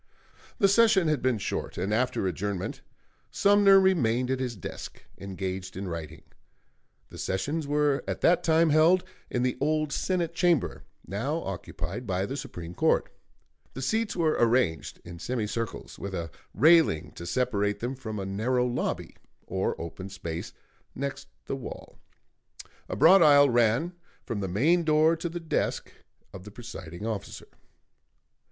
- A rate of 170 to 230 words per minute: No, average, 150 wpm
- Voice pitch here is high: No, low, 125 Hz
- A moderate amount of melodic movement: No, wide, 8.3 semitones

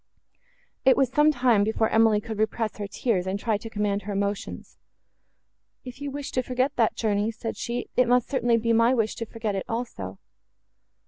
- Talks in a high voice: Yes, high, 225 Hz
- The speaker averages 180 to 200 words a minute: Yes, average, 190 wpm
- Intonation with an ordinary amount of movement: Yes, average, 3.0 semitones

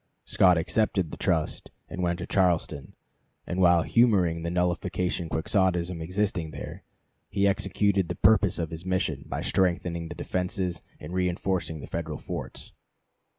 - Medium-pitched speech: No, very low, 90 Hz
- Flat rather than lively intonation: Yes, narrow, 2.0 semitones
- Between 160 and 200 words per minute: No, average, 145 wpm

